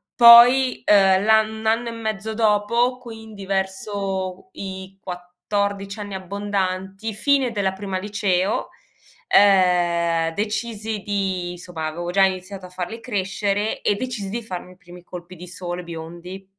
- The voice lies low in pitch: No, high, 195 Hz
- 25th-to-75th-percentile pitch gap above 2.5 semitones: Yes, average, 2.9 semitones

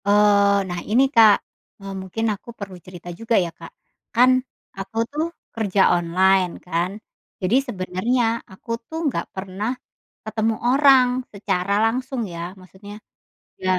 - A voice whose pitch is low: No, high, 200 Hz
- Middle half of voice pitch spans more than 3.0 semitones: Yes, average, 3.8 semitones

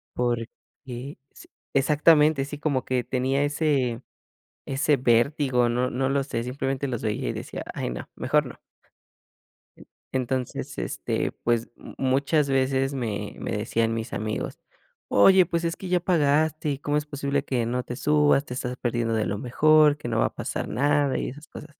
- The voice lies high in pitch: No, low, 135 Hz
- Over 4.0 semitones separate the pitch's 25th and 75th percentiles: No, average, 3.3 semitones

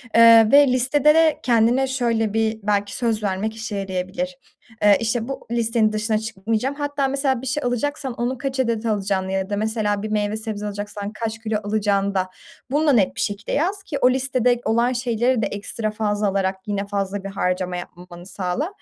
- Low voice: No, high, 220 Hz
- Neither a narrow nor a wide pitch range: Yes, average, 3.8 semitones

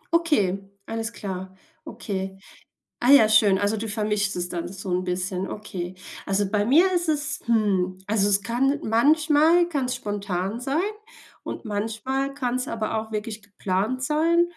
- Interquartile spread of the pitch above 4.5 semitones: Yes, wide, 5.5 semitones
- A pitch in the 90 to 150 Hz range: No, high, 215 Hz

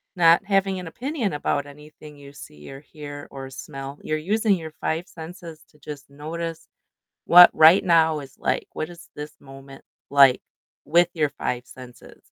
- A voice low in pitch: No, medium, 155 Hz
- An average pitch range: Yes, average, 3.3 semitones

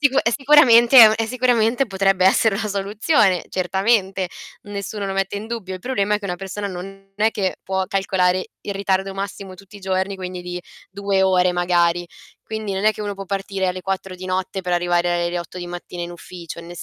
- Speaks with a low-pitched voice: No, high, 195 Hz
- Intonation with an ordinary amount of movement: No, narrow, 2.2 semitones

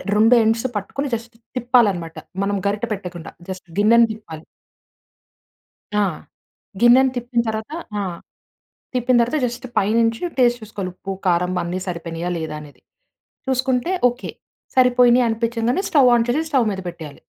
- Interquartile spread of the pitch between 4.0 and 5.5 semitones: Yes, average, 4.7 semitones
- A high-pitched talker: Yes, high, 225 Hz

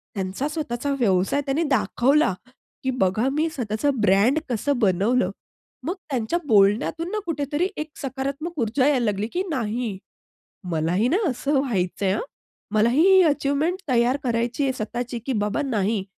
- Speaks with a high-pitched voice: Yes, very high, 250 Hz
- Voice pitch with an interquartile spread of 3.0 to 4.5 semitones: No, average, 5.2 semitones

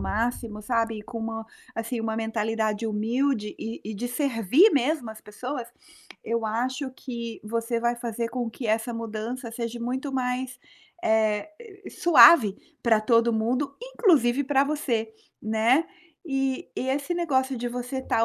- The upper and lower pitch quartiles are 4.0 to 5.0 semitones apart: No, average, 2.8 semitones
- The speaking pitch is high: Yes, high, 235 Hz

